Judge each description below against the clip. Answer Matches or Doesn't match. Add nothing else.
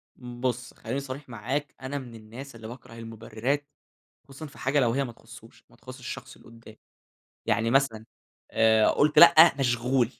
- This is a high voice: Doesn't match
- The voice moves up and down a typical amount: Matches